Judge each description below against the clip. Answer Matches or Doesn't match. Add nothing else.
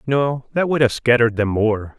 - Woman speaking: Doesn't match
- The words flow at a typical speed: Doesn't match